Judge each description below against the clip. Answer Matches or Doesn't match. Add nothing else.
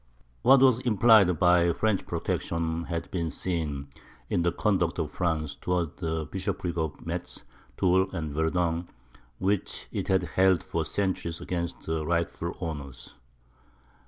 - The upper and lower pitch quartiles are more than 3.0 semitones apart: Doesn't match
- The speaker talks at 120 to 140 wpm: Matches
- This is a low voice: Matches